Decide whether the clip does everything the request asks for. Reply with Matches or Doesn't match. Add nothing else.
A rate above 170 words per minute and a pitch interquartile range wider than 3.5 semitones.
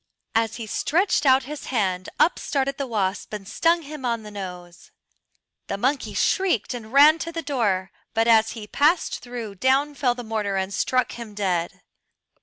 Matches